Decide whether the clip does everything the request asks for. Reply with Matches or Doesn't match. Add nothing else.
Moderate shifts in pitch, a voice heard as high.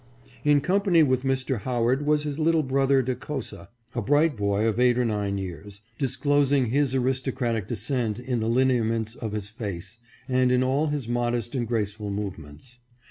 Doesn't match